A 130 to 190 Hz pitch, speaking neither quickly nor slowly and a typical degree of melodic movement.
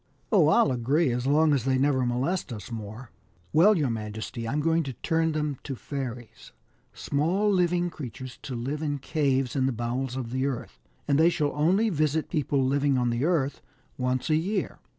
Yes: medium, 140 Hz; average, 195 wpm; average, 4.0 semitones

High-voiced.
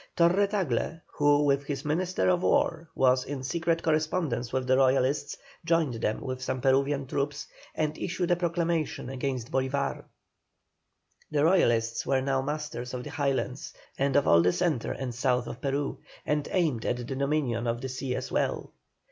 No: medium, 140 Hz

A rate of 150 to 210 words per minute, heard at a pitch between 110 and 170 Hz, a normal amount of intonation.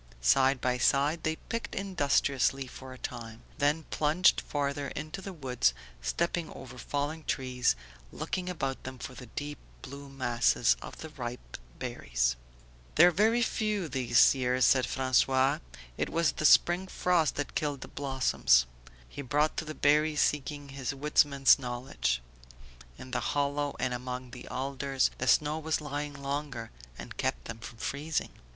Yes: average, 155 wpm; medium, 140 Hz; average, 3.1 semitones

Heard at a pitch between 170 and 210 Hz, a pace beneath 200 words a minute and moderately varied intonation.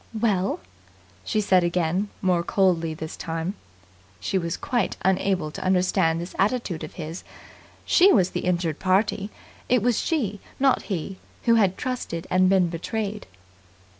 Yes: medium, 185 Hz; average, 145 wpm; average, 3.4 semitones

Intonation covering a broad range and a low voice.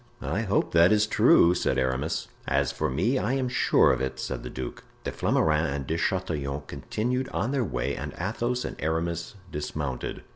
Yes: wide, 7.7 semitones; very low, 80 Hz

